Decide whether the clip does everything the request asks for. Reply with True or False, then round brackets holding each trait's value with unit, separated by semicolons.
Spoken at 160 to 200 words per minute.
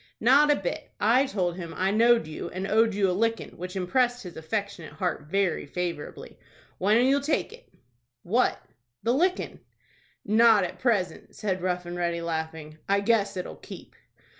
True (165 wpm)